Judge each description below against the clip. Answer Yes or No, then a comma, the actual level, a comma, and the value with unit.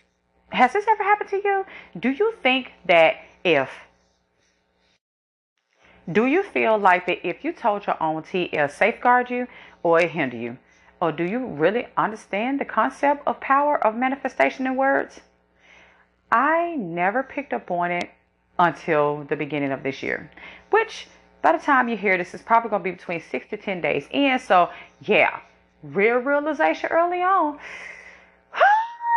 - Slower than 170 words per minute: Yes, average, 160 wpm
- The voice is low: No, high, 205 Hz